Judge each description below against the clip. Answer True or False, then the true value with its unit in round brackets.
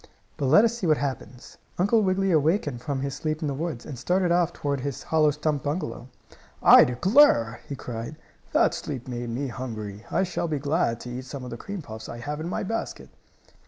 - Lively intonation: True (5.7 semitones)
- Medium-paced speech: False (210 wpm)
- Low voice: False (145 Hz)